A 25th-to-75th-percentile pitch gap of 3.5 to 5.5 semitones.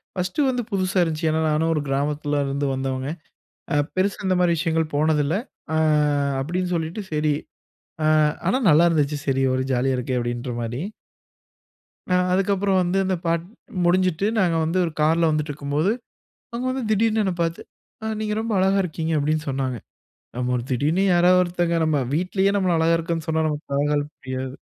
Yes: average, 4.1 semitones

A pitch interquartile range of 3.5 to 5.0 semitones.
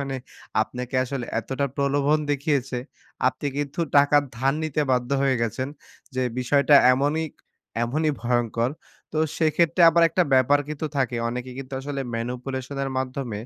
No: narrow, 2.4 semitones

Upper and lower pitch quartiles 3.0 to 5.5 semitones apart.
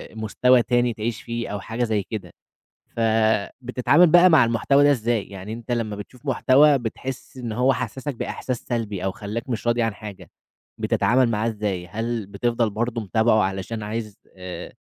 No: narrow, 2.6 semitones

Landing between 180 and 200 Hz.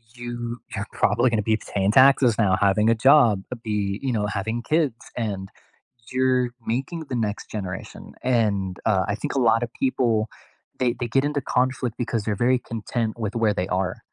No: low, 115 Hz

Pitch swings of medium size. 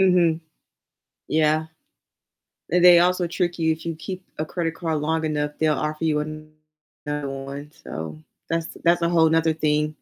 No: narrow, 1.8 semitones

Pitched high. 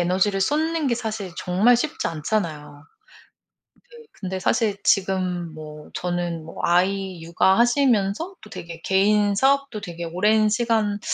Yes: high, 195 Hz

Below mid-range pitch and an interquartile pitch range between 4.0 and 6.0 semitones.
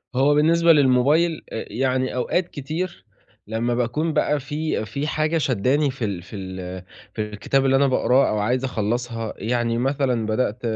Yes: low, 130 Hz; average, 4.4 semitones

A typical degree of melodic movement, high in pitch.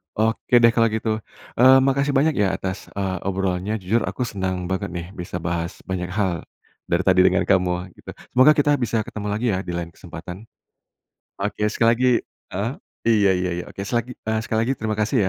No: average, 4.1 semitones; low, 105 Hz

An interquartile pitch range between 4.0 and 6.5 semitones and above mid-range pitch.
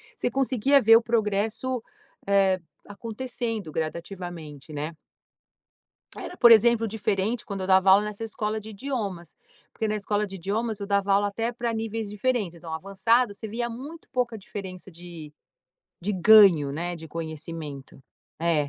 Yes: average, 4.5 semitones; high, 205 Hz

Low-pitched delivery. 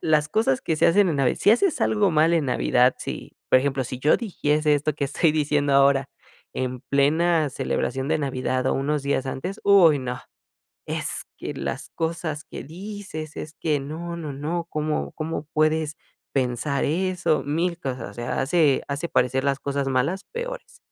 No: medium, 150 Hz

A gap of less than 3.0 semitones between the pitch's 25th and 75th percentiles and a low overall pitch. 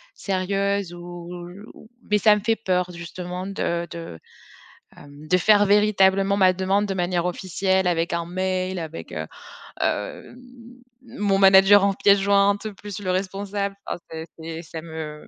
No: narrow, 2.5 semitones; medium, 185 Hz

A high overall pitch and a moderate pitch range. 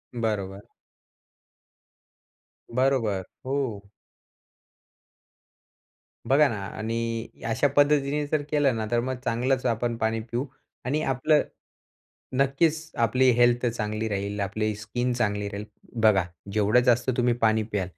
No: low, 120 Hz; average, 3.5 semitones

